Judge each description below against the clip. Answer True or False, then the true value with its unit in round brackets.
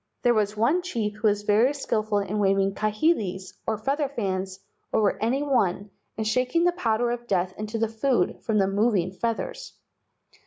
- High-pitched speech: True (215 Hz)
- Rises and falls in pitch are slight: False (3.3 semitones)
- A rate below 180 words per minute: True (170 wpm)